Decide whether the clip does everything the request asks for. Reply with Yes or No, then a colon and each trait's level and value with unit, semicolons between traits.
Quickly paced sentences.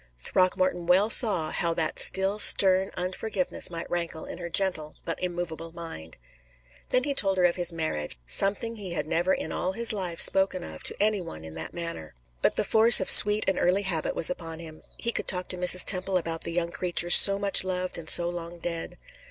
Yes: fast, 210 wpm